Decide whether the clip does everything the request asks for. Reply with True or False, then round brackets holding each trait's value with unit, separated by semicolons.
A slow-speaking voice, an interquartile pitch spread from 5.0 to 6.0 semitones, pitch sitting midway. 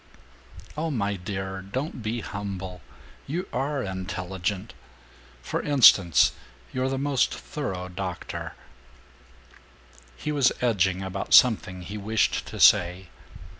False (115 wpm; 5.6 semitones; 100 Hz)